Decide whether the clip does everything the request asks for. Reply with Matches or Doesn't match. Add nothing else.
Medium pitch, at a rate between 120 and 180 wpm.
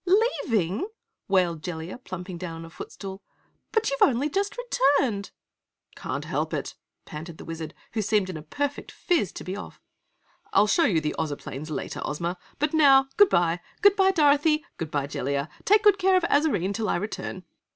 Doesn't match